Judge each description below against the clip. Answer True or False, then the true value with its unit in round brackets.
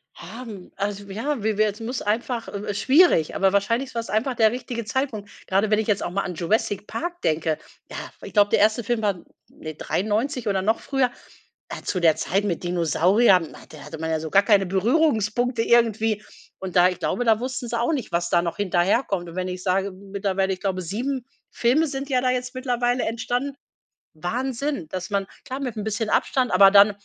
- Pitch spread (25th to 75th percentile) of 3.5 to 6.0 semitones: True (4.3 semitones)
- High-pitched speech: True (210 Hz)